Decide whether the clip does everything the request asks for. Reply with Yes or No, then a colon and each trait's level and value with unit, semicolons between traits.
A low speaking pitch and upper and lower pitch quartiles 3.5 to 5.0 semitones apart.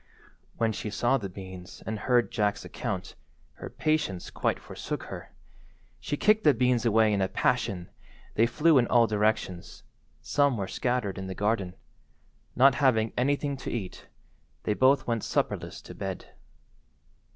Yes: low, 115 Hz; average, 4.3 semitones